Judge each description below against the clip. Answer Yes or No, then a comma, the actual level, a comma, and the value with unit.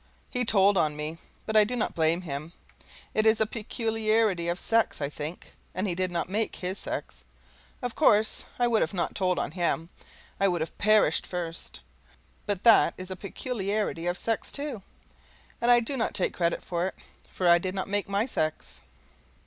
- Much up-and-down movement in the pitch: No, average, 4.2 semitones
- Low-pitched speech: No, high, 195 Hz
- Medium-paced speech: Yes, average, 190 wpm